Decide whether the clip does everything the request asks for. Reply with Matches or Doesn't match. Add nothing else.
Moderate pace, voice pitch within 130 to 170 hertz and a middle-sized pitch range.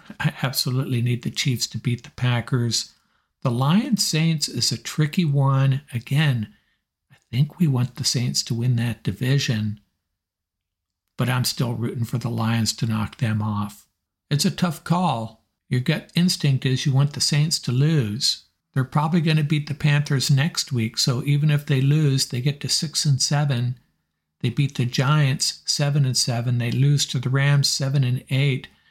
Matches